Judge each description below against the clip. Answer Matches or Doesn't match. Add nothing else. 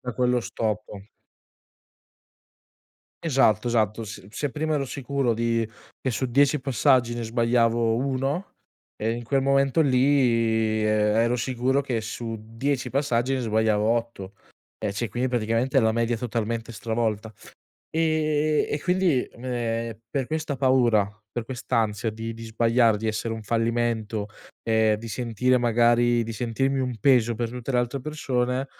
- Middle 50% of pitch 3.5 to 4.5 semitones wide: Doesn't match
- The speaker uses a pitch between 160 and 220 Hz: Doesn't match